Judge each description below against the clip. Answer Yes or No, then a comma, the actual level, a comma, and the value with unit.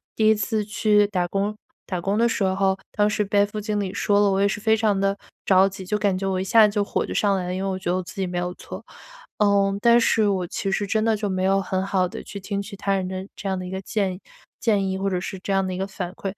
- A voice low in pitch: No, high, 195 Hz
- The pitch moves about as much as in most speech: No, narrow, 1.7 semitones